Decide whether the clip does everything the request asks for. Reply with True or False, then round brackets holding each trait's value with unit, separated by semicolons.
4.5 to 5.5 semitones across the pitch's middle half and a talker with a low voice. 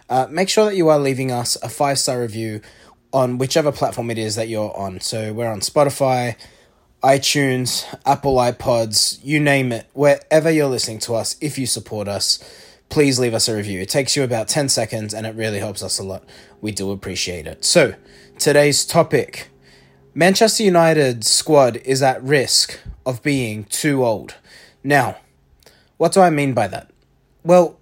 True (4.8 semitones; 125 Hz)